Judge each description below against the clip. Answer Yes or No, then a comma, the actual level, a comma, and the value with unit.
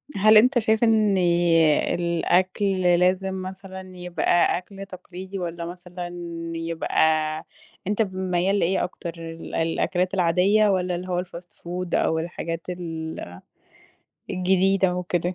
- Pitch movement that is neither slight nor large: No, narrow, 1.7 semitones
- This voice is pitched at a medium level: Yes, medium, 180 Hz